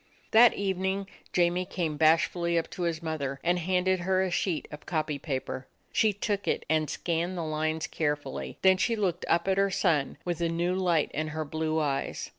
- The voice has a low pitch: No, medium, 170 Hz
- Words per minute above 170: Yes, average, 200 wpm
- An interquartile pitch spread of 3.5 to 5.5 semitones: No, average, 3.1 semitones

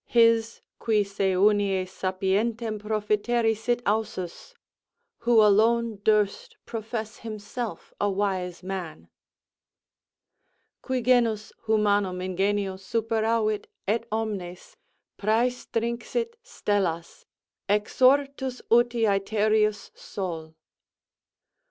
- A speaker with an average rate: No, slow, 80 wpm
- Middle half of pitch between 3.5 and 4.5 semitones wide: No, average, 2.8 semitones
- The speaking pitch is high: Yes, high, 215 Hz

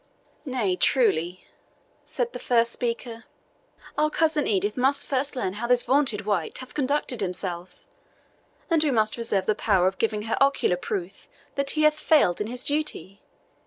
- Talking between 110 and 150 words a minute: No, average, 160 wpm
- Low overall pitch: No, high, 235 Hz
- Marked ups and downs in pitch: Yes, wide, 6.0 semitones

